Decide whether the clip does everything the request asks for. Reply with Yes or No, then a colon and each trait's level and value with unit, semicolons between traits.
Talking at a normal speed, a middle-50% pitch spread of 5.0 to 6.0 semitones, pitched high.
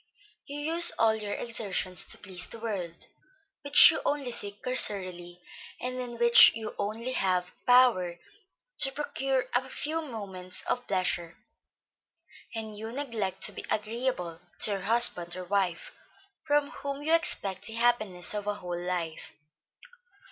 Yes: average, 145 wpm; wide, 5.5 semitones; high, 220 Hz